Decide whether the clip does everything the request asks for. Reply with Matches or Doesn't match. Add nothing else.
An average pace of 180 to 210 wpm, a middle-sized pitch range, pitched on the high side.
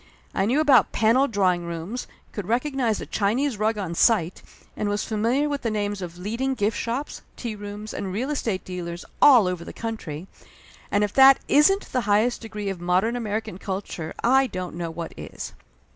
Matches